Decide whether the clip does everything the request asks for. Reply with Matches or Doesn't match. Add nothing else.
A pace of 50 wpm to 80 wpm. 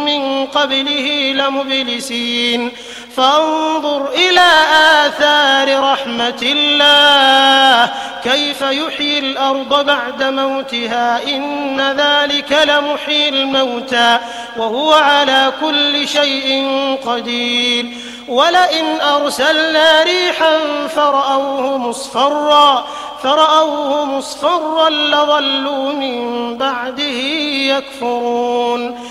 Matches